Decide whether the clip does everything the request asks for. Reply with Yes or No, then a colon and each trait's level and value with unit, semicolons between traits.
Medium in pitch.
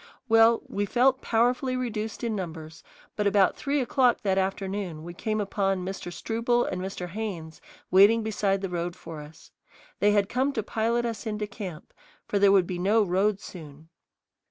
No: high, 200 Hz